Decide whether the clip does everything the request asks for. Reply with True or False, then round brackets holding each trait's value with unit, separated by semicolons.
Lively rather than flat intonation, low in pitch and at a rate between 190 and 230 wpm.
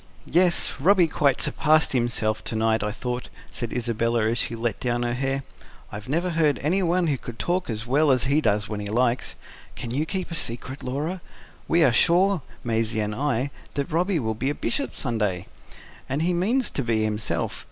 True (6.1 semitones; 130 Hz; 195 wpm)